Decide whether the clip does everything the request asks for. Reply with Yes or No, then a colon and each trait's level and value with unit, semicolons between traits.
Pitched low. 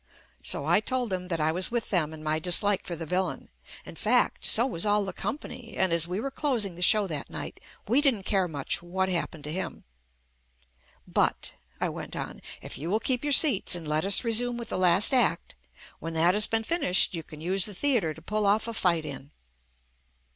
No: high, 190 Hz